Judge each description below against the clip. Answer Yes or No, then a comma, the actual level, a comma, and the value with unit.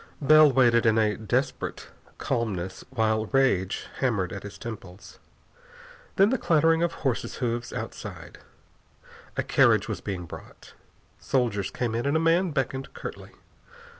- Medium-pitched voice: No, low, 120 Hz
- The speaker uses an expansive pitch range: No, average, 5.0 semitones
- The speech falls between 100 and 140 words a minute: Yes, slow, 135 wpm